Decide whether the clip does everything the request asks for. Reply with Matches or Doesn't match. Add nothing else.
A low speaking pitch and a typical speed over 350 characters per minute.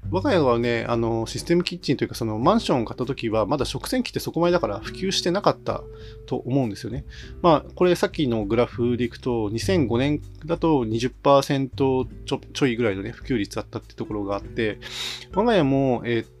Matches